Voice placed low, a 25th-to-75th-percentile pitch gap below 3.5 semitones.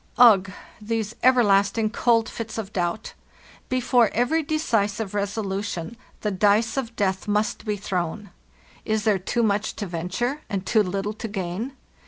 No: high, 210 Hz; average, 2.7 semitones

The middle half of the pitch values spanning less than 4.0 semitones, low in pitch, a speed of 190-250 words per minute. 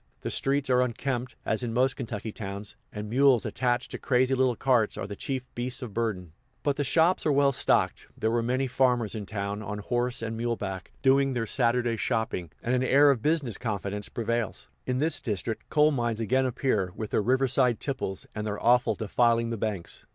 Yes: average, 3.3 semitones; low, 120 Hz; average, 200 wpm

